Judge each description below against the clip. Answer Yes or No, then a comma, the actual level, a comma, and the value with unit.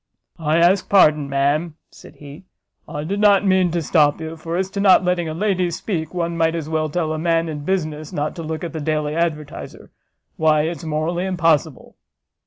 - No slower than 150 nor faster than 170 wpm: No, average, 195 wpm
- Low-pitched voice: No, medium, 165 Hz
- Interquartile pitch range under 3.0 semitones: Yes, narrow, 2.5 semitones